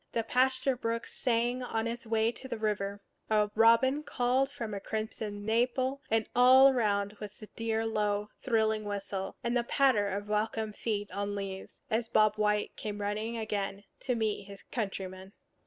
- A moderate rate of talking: Yes, average, 170 wpm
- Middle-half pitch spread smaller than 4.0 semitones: Yes, narrow, 2.5 semitones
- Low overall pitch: No, high, 220 Hz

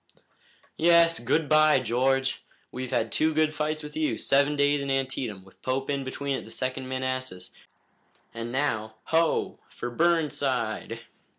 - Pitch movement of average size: Yes, average, 3.5 semitones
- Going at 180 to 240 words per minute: No, average, 150 wpm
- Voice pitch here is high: No, low, 135 Hz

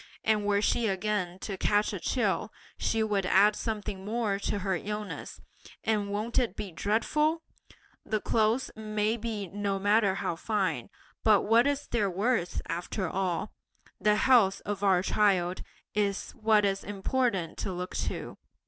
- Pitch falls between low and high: No, high, 205 Hz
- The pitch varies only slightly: Yes, narrow, 2.1 semitones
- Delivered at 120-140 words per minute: No, average, 155 wpm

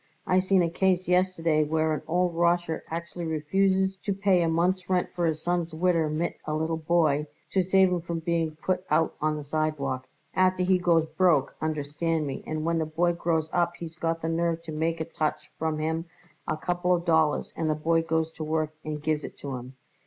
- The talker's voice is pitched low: No, medium, 165 Hz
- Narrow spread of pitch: Yes, narrow, 2.1 semitones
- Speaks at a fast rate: Yes, fast, 210 wpm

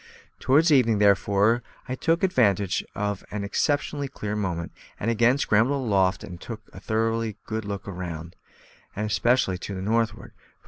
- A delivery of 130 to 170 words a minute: Yes, average, 155 wpm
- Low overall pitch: Yes, low, 105 Hz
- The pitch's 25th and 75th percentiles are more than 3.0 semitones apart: Yes, average, 3.4 semitones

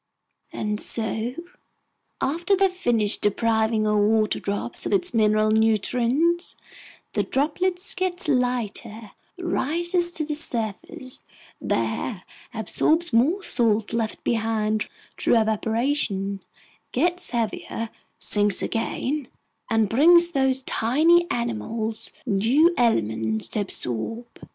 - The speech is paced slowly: Yes, slow, 105 wpm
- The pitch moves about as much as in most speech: No, wide, 6.2 semitones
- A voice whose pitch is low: No, high, 235 Hz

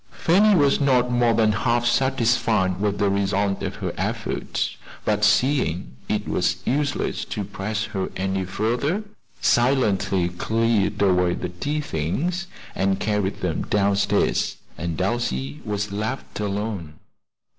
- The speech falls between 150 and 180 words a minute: No, slow, 135 wpm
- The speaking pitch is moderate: No, low, 105 Hz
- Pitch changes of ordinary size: Yes, average, 4.1 semitones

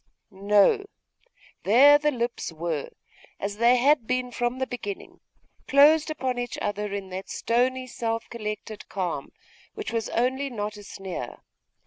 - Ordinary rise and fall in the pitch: Yes, average, 4.0 semitones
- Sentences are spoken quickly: No, average, 140 wpm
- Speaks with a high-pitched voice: Yes, high, 235 Hz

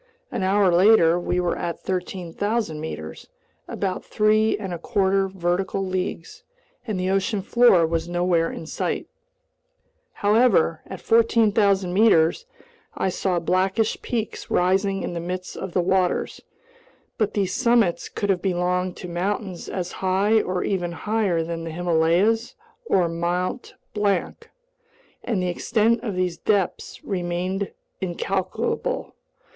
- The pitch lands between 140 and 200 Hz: Yes, medium, 185 Hz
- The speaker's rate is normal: No, slow, 130 wpm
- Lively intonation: No, average, 2.8 semitones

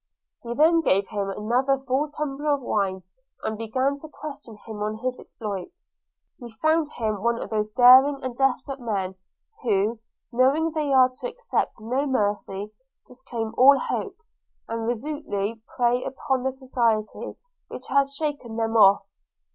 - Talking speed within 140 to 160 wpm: Yes, average, 150 wpm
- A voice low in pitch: No, very high, 250 Hz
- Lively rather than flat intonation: No, average, 4.2 semitones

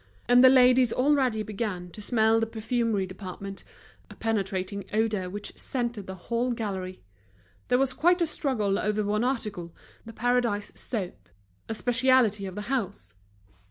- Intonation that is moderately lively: Yes, average, 3.8 semitones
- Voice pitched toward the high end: Yes, high, 220 Hz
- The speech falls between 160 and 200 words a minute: No, average, 150 wpm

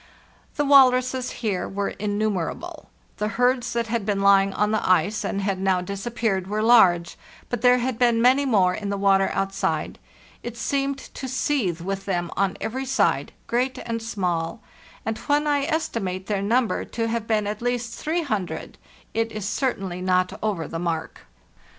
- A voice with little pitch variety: No, average, 4.2 semitones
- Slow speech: No, average, 170 wpm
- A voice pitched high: Yes, high, 215 Hz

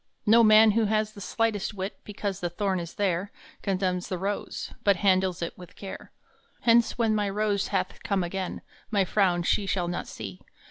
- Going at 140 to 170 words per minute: No, average, 185 wpm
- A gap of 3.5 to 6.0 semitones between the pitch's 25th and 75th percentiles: No, average, 2.7 semitones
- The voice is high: Yes, high, 195 Hz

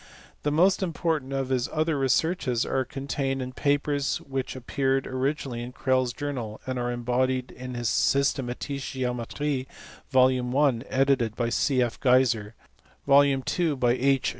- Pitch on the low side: Yes, low, 130 Hz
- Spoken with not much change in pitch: Yes, narrow, 2.1 semitones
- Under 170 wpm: Yes, average, 155 wpm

